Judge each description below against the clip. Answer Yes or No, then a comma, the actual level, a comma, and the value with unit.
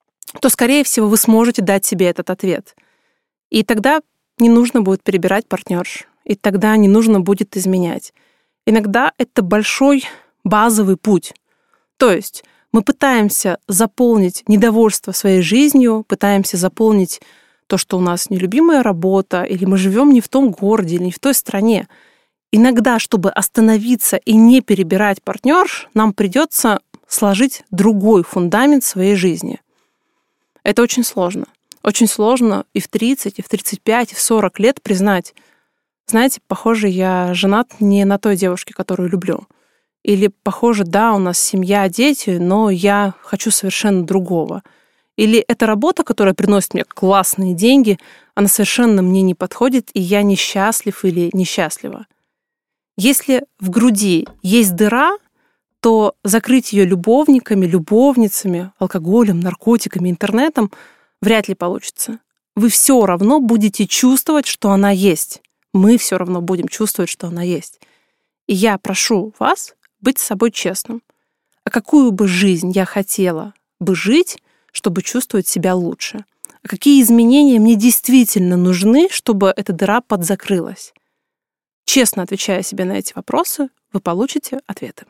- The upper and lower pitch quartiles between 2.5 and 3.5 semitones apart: No, average, 4.0 semitones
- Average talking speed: Yes, average, 140 wpm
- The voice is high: Yes, high, 215 Hz